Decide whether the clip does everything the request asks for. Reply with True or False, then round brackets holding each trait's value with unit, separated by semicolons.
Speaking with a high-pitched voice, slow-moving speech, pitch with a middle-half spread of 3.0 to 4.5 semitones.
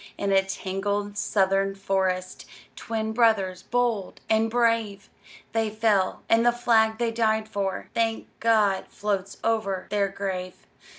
False (205 Hz; 130 wpm; 2.6 semitones)